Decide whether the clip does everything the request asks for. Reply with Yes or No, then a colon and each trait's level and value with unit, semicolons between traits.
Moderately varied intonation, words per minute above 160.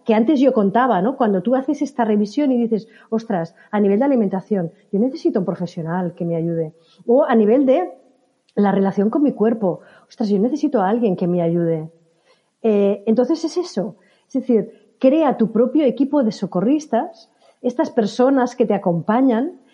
Yes: average, 4.9 semitones; average, 175 wpm